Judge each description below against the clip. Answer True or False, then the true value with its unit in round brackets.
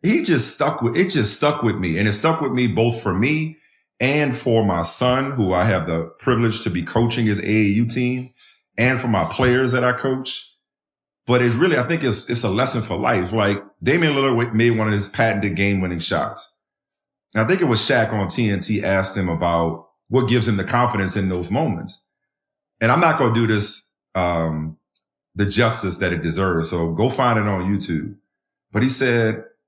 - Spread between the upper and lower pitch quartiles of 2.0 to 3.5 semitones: False (4.4 semitones)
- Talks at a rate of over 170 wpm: True (205 wpm)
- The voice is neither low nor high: False (110 Hz)